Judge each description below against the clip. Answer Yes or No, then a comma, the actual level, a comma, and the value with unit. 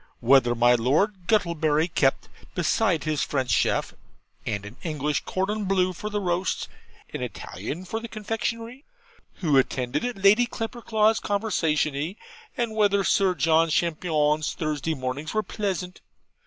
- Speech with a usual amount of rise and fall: No, wide, 5.8 semitones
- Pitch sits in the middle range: Yes, medium, 175 Hz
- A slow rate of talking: Yes, slow, 130 wpm